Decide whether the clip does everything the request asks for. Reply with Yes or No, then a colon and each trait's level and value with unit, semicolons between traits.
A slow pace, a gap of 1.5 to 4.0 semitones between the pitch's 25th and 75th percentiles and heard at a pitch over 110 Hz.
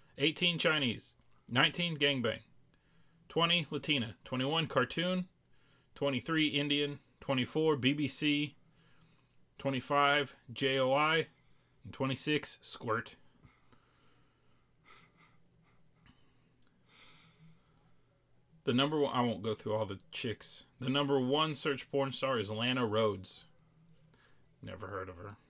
Yes: slow, 95 wpm; average, 3.2 semitones; medium, 140 Hz